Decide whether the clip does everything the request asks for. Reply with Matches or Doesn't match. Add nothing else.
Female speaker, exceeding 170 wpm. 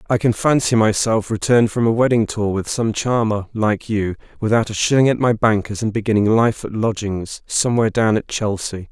Doesn't match